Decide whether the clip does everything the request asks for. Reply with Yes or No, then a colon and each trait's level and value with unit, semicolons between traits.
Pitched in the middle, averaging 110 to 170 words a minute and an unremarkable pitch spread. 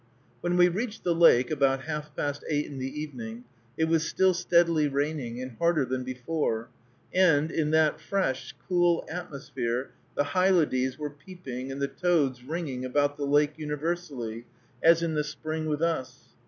Yes: medium, 150 Hz; average, 165 wpm; average, 4.2 semitones